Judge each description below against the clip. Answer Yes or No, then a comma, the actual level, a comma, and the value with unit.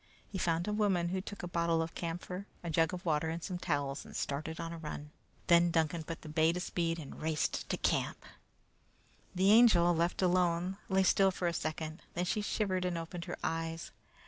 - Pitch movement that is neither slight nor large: No, narrow, 1.9 semitones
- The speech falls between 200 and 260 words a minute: Yes, fast, 205 wpm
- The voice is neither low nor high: Yes, medium, 170 Hz